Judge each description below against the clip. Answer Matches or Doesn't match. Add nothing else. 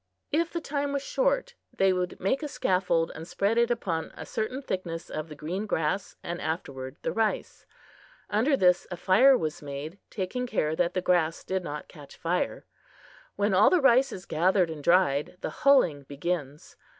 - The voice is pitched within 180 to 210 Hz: Matches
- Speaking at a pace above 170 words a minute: Matches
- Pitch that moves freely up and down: Matches